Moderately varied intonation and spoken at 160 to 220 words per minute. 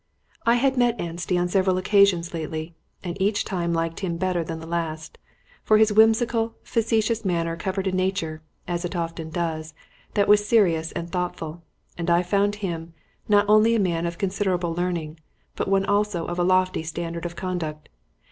Yes: average, 3.4 semitones; average, 175 wpm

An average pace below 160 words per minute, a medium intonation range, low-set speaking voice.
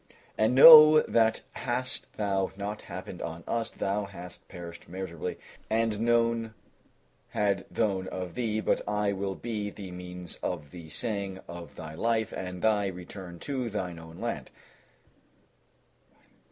Yes: average, 140 wpm; average, 3.9 semitones; low, 100 Hz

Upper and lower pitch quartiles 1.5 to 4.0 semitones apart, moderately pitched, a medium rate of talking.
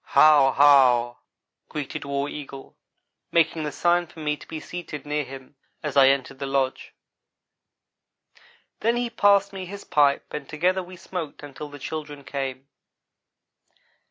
Yes: average, 3.7 semitones; medium, 150 Hz; average, 145 wpm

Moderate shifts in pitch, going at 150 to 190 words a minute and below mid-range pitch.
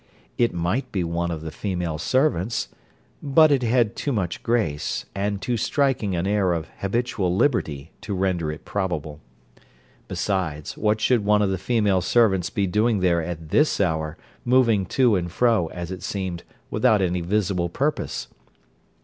Yes: average, 4.9 semitones; average, 160 wpm; very low, 95 Hz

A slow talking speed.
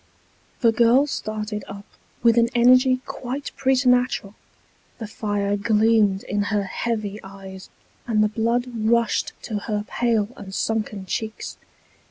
Yes: slow, 130 wpm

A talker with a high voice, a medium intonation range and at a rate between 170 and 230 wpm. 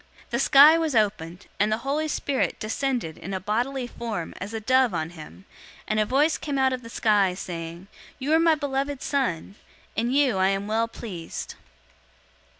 No: high, 230 Hz; wide, 5.9 semitones; average, 185 wpm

